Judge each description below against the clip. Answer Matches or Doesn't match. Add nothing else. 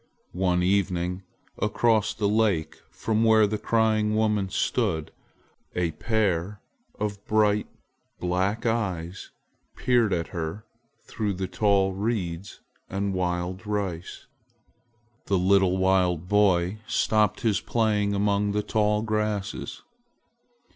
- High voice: Doesn't match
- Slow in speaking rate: Matches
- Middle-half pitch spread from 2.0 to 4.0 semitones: Matches